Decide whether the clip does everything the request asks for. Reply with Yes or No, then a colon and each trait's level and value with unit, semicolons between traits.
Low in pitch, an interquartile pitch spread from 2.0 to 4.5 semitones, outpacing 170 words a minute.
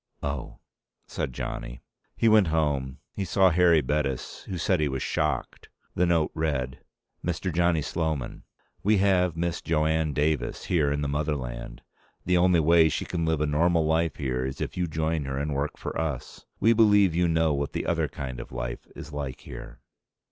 Yes: very low, 80 Hz; average, 3.5 semitones; average, 185 wpm